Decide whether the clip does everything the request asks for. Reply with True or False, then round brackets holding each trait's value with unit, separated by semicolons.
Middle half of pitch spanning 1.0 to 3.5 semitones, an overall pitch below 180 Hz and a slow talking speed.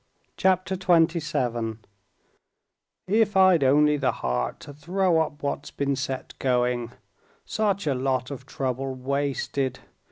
False (5.0 semitones; 140 Hz; 120 wpm)